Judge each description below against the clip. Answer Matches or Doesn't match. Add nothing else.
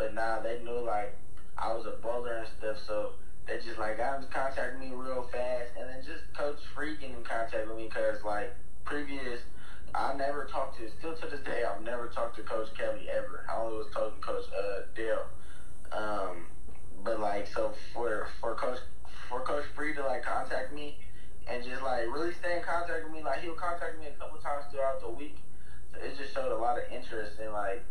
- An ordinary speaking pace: Doesn't match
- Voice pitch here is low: Matches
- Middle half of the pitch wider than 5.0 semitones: Matches